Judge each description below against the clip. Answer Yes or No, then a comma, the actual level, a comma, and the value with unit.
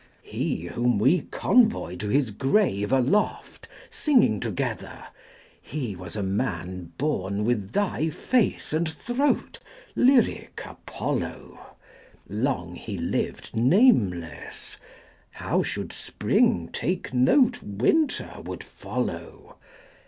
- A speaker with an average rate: No, slow, 110 wpm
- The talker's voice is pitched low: Yes, low, 130 Hz